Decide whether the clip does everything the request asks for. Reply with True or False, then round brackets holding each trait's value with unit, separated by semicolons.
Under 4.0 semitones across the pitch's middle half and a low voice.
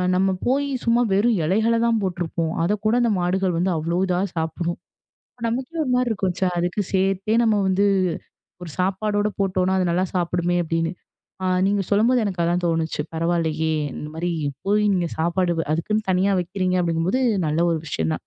False (3.3 semitones; 185 Hz)